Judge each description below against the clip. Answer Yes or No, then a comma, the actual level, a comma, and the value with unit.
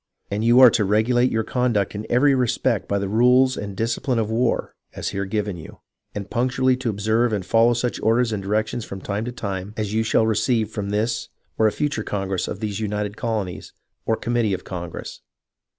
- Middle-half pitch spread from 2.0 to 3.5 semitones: Yes, average, 2.9 semitones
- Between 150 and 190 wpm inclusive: No, average, 200 wpm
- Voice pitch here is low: Yes, low, 110 Hz